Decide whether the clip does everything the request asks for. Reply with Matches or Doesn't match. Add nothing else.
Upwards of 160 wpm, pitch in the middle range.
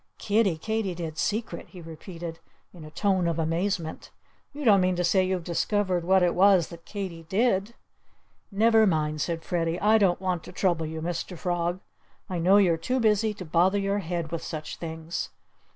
Matches